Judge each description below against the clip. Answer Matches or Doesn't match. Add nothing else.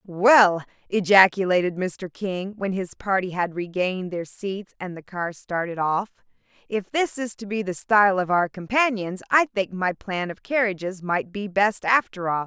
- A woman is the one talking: Matches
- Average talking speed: Matches